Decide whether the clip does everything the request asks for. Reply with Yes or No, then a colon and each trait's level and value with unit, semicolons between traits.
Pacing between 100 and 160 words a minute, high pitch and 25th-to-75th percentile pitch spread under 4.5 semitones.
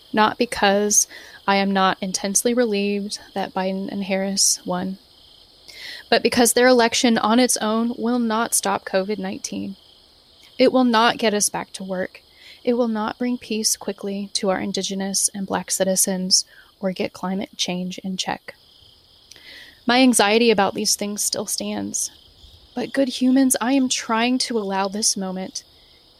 Yes: average, 155 wpm; high, 205 Hz; average, 3.8 semitones